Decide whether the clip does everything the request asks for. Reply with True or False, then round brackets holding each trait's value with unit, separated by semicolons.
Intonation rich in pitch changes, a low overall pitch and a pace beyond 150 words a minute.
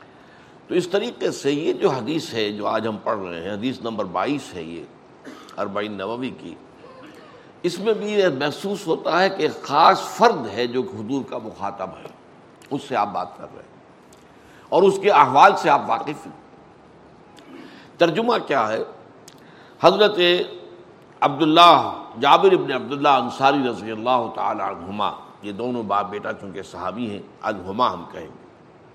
True (8.7 semitones; 130 Hz; 160 wpm)